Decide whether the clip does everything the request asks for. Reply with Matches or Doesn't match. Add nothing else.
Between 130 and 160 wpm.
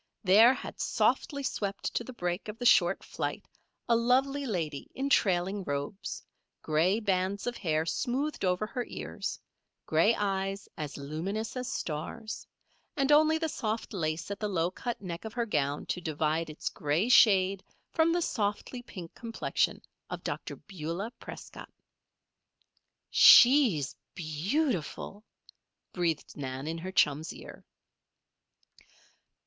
Matches